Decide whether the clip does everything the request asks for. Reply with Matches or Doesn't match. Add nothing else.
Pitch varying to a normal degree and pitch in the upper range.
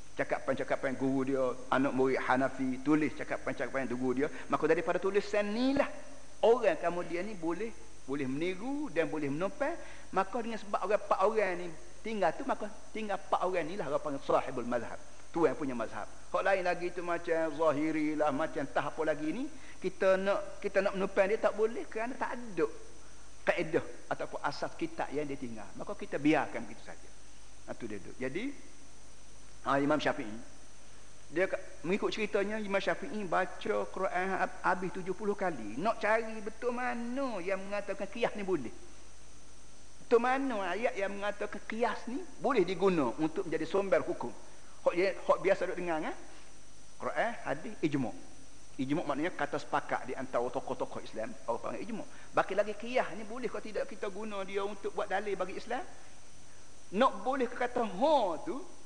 Doesn't match